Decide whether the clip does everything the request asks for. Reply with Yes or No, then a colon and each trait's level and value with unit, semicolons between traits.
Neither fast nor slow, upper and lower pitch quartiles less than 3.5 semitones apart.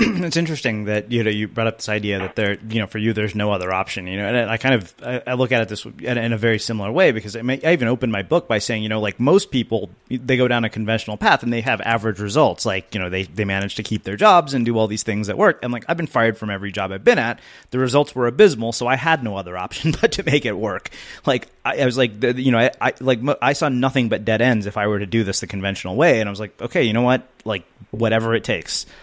No: fast, 295 wpm; average, 3.1 semitones